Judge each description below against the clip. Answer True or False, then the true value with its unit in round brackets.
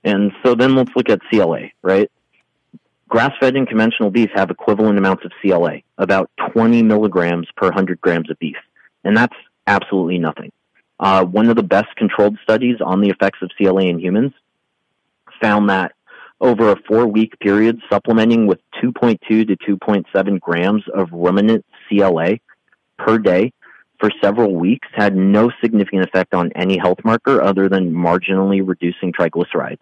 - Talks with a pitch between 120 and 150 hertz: False (100 Hz)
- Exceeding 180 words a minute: False (155 wpm)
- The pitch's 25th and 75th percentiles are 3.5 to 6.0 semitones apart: False (3.0 semitones)